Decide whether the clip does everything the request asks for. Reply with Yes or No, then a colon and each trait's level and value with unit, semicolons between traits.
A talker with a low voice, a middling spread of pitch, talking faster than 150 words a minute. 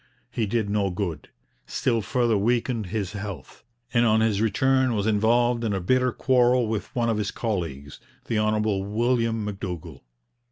Yes: low, 110 Hz; average, 3.0 semitones; average, 160 wpm